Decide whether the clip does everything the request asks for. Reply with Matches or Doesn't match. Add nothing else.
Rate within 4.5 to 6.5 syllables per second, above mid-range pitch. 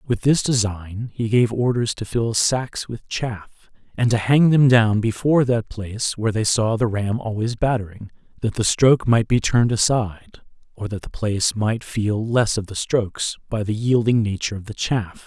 Doesn't match